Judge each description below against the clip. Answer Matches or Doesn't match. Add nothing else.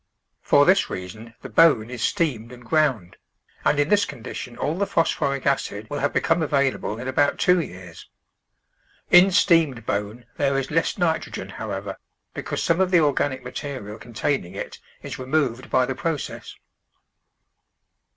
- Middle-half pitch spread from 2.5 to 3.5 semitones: Doesn't match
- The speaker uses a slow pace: Doesn't match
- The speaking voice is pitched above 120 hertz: Matches